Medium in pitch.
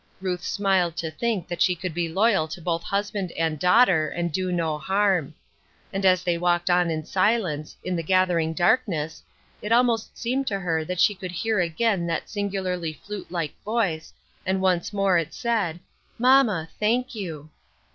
Yes: medium, 180 Hz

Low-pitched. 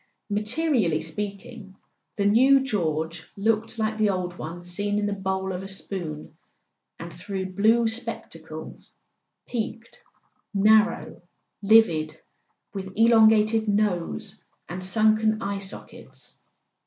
No: high, 205 Hz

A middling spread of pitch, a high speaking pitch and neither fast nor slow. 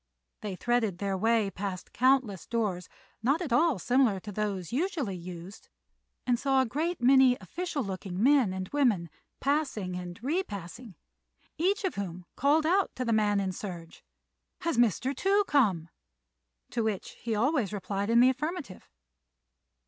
No: wide, 6.2 semitones; high, 230 Hz; average, 150 wpm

